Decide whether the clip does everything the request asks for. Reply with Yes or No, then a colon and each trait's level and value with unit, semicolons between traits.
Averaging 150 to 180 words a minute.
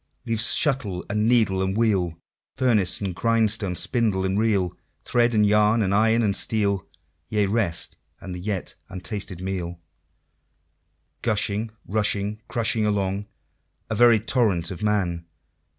No: slow, 135 wpm